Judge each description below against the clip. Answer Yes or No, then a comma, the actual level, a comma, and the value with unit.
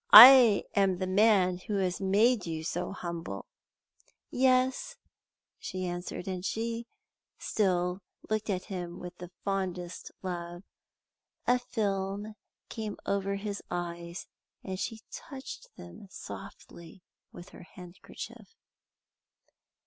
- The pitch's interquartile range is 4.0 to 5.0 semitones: No, average, 3.3 semitones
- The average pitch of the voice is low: No, high, 190 Hz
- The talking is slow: Yes, slow, 110 wpm